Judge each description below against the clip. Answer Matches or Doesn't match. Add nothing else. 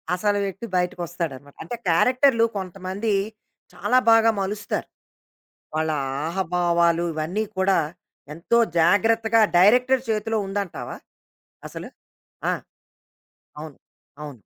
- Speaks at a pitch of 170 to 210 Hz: Matches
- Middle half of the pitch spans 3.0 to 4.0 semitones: Doesn't match